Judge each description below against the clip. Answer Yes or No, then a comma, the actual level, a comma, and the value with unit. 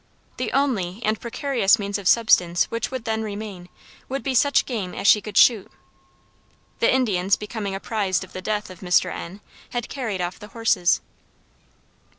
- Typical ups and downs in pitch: Yes, average, 3.7 semitones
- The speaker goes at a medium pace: Yes, average, 165 wpm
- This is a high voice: Yes, high, 210 Hz